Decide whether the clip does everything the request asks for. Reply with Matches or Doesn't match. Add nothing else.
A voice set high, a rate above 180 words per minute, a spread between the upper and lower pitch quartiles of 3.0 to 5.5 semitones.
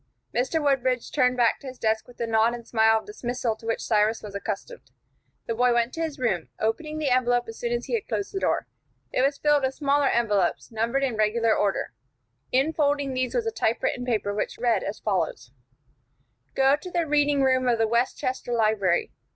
Matches